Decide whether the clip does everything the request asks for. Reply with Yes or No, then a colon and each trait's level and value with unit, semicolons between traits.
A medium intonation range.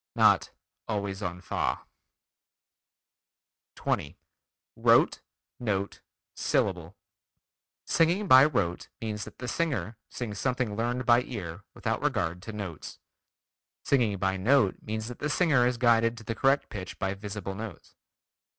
Yes: average, 4.2 semitones